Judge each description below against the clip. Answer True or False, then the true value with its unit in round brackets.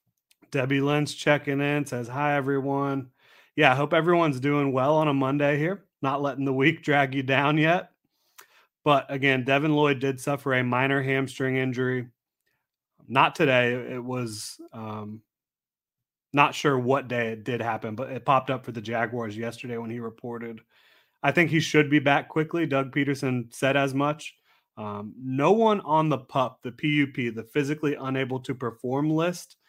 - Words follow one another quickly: False (170 wpm)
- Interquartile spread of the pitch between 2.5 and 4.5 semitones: True (2.8 semitones)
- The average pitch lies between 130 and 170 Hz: True (135 Hz)